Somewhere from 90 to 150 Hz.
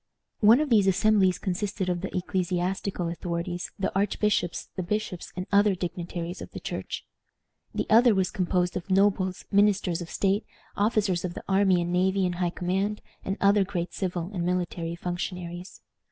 No: medium, 185 Hz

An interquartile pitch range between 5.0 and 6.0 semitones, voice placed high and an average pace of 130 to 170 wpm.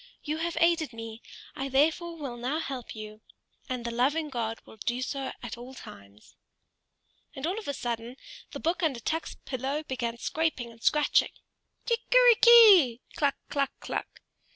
Yes: average, 5.3 semitones; very high, 270 Hz; average, 160 wpm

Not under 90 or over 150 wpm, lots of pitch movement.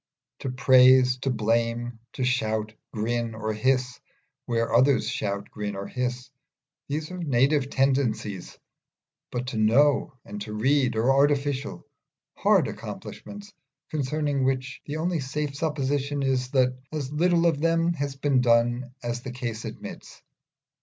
No: average, 140 wpm; average, 3.2 semitones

